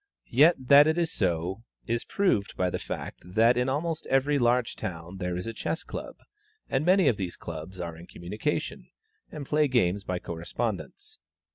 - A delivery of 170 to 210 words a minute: Yes, average, 175 wpm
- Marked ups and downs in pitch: Yes, wide, 8.2 semitones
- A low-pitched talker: Yes, low, 115 Hz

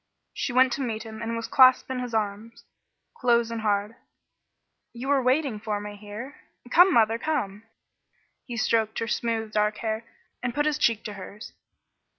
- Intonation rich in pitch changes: No, average, 2.9 semitones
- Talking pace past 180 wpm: No, average, 170 wpm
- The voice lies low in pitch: No, high, 230 Hz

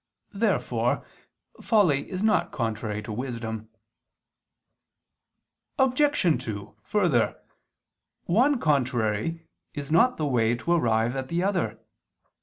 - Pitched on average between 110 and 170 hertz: Yes, medium, 140 Hz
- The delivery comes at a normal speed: No, slow, 100 wpm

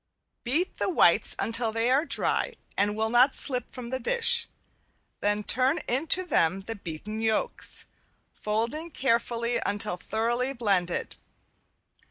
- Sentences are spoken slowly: Yes, slow, 130 wpm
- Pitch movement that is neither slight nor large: Yes, average, 3.6 semitones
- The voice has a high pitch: Yes, high, 235 Hz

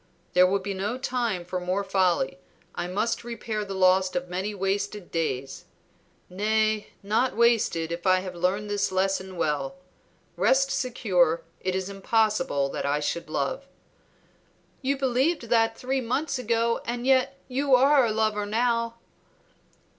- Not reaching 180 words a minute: Yes, average, 145 wpm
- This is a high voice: Yes, high, 205 Hz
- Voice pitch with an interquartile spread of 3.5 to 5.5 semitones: Yes, average, 4.3 semitones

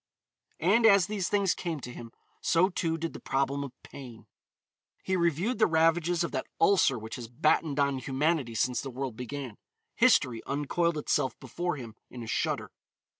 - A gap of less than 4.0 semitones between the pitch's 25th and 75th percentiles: No, wide, 5.4 semitones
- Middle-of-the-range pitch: Yes, medium, 150 Hz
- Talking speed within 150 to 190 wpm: Yes, average, 175 wpm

